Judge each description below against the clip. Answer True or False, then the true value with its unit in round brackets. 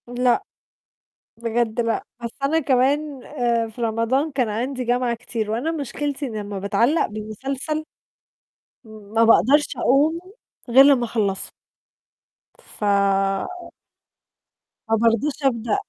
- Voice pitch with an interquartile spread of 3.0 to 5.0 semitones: True (3.6 semitones)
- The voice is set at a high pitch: True (240 Hz)